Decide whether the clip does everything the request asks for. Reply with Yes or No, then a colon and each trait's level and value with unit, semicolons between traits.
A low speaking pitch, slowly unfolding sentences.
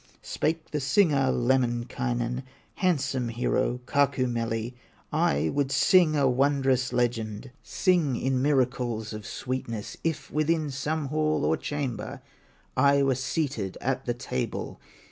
Yes: low, 130 Hz; slow, 120 wpm